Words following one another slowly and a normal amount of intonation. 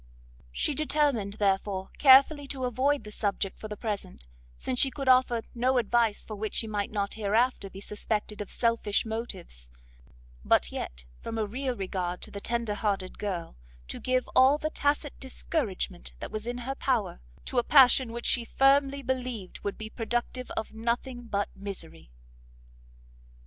No: average, 165 wpm; average, 4.2 semitones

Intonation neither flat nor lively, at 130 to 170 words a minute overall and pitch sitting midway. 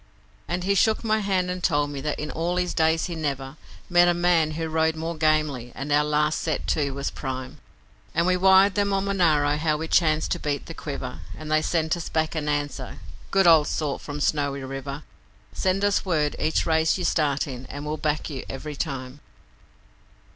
No: average, 3.1 semitones; fast, 205 wpm; medium, 155 Hz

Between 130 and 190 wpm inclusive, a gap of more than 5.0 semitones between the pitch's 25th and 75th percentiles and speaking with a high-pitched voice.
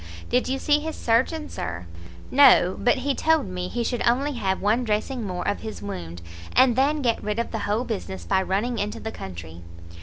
No: fast, 205 wpm; wide, 5.4 semitones; high, 225 Hz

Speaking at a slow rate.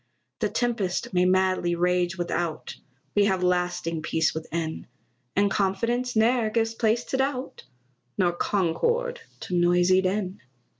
Yes: slow, 130 wpm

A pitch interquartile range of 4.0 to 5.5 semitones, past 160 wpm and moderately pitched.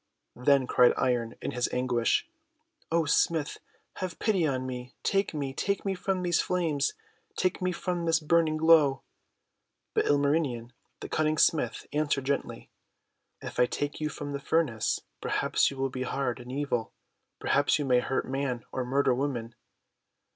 Yes: average, 4.3 semitones; average, 170 wpm; medium, 145 Hz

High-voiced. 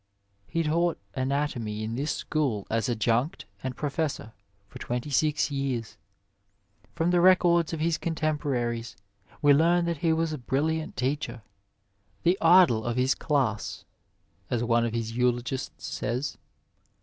No: medium, 140 Hz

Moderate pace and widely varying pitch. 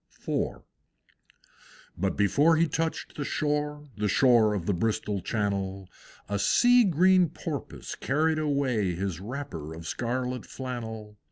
No: slow, 125 wpm; wide, 6.6 semitones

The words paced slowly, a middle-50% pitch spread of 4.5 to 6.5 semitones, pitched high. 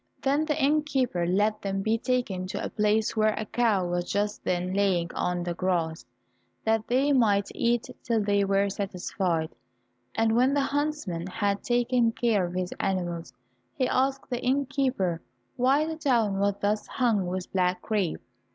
No: average, 165 wpm; average, 5.2 semitones; high, 210 Hz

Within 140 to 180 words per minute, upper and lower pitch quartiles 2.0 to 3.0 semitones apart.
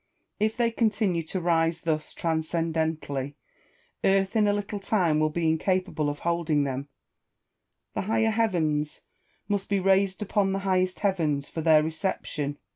No: average, 145 wpm; average, 4.0 semitones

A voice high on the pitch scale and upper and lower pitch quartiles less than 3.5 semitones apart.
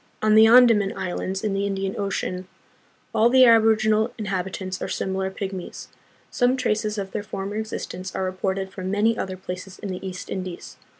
Yes: high, 195 Hz; narrow, 2.5 semitones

